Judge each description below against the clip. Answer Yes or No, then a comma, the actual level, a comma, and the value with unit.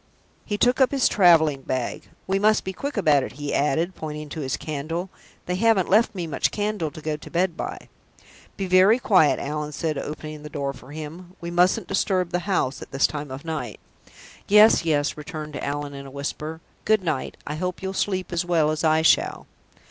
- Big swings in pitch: No, average, 4.0 semitones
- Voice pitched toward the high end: No, medium, 160 Hz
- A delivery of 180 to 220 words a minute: Yes, fast, 205 wpm